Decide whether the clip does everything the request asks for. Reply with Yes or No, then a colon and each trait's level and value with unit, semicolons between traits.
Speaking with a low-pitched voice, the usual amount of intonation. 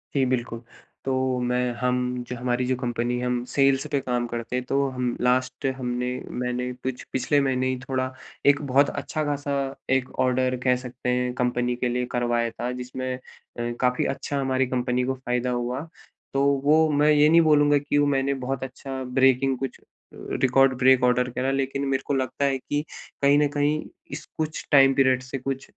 No: low, 130 Hz; narrow, 1.6 semitones